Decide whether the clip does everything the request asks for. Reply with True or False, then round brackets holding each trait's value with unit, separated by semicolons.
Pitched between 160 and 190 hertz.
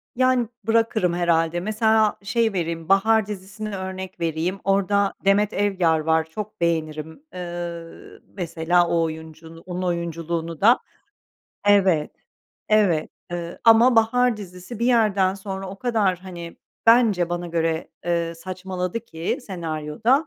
True (185 Hz)